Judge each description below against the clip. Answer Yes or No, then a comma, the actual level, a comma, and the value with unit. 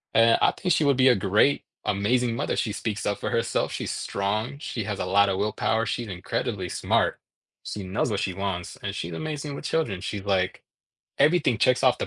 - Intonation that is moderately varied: Yes, average, 4.3 semitones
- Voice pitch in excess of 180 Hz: No, low, 105 Hz